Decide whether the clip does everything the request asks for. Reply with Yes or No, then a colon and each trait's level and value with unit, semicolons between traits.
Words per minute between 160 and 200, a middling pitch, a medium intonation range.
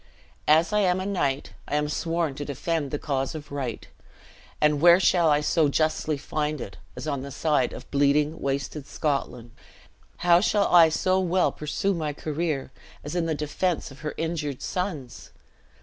Yes: average, 175 wpm; medium, 150 Hz; average, 3.2 semitones